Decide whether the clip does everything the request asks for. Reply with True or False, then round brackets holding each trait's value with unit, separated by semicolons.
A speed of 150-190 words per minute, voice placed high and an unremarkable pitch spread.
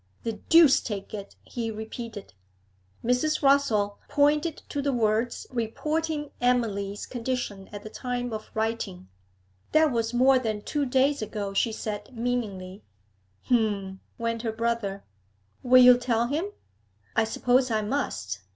False (135 wpm; 235 Hz; 3.5 semitones)